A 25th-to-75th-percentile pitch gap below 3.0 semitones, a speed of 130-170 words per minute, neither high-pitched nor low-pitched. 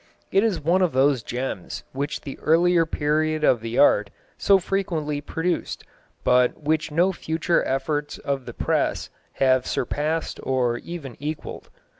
No: average, 3.8 semitones; average, 145 wpm; medium, 150 Hz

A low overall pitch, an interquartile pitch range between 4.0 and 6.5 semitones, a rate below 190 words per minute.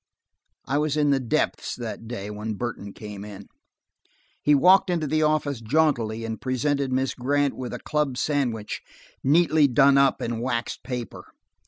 Yes: low, 130 Hz; average, 4.3 semitones; average, 160 wpm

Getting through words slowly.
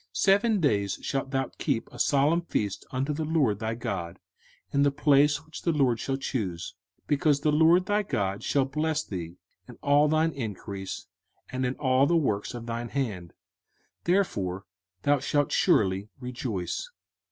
No: average, 165 wpm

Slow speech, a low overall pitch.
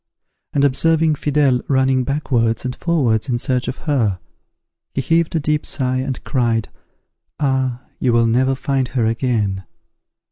No: average, 145 wpm; low, 130 Hz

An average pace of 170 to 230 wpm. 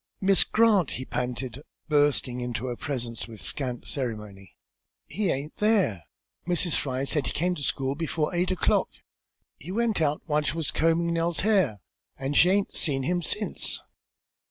No: average, 160 wpm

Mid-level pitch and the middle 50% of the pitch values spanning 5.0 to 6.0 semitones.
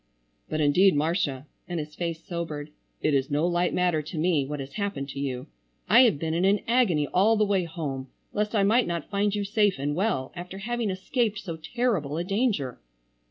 Yes: medium, 175 Hz; wide, 5.5 semitones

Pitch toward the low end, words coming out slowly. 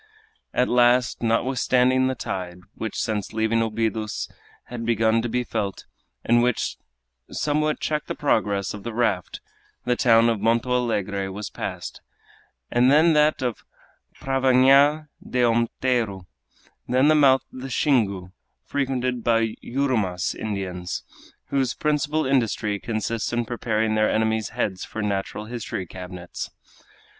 Yes: low, 115 Hz; slow, 130 wpm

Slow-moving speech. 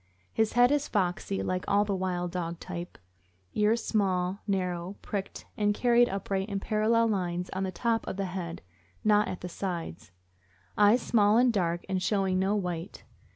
No: average, 170 wpm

